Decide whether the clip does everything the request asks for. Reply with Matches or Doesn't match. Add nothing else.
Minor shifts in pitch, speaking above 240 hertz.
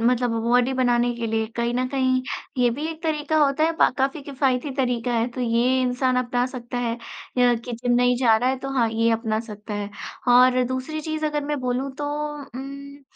Matches